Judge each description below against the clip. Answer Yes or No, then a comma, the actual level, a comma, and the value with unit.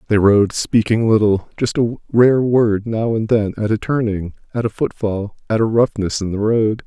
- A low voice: Yes, low, 110 Hz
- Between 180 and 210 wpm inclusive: Yes, average, 200 wpm